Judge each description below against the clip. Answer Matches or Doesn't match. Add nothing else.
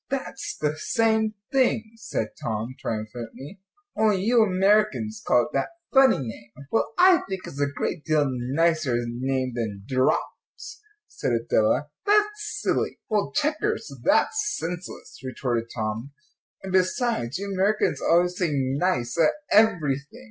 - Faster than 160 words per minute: Doesn't match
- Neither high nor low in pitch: Matches